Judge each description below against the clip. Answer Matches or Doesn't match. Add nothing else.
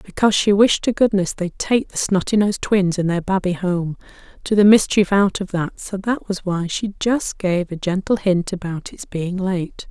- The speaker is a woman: Matches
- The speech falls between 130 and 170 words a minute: Doesn't match